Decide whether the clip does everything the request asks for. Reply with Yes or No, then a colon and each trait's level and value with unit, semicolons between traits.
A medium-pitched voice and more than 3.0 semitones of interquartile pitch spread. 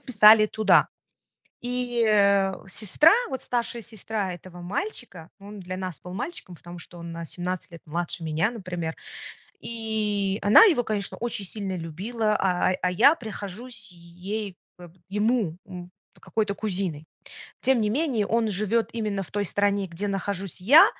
No: high, 200 Hz; average, 3.7 semitones